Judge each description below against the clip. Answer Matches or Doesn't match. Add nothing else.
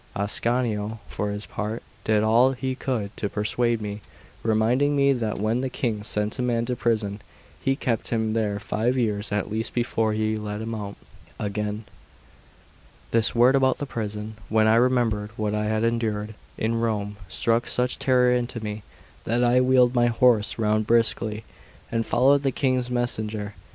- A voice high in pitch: Doesn't match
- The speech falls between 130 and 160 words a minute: Doesn't match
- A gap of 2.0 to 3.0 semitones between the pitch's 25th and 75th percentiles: Matches